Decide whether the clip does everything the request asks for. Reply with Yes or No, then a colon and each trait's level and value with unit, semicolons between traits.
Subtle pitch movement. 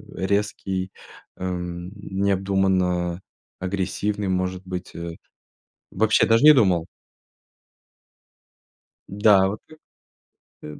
Yes: narrow, 1.9 semitones